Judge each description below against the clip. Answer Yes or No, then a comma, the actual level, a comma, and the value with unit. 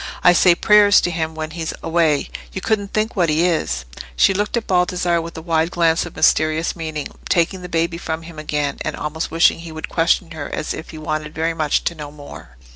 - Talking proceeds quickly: Yes, fast, 220 wpm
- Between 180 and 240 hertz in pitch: No, medium, 165 Hz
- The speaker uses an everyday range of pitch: No, narrow, 2.0 semitones